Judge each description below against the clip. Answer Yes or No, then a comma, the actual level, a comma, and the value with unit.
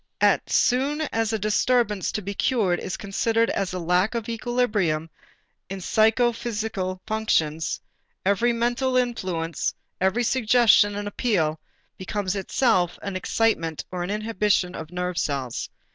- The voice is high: Yes, high, 205 Hz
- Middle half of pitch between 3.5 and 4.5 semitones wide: Yes, average, 4.2 semitones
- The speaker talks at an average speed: No, slow, 130 wpm